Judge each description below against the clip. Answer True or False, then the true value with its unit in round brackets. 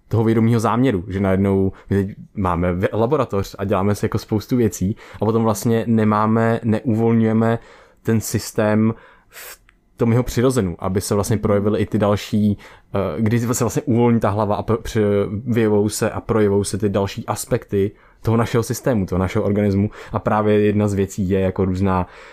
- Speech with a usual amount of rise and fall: False (2.2 semitones)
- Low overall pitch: True (105 Hz)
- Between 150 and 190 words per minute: True (165 wpm)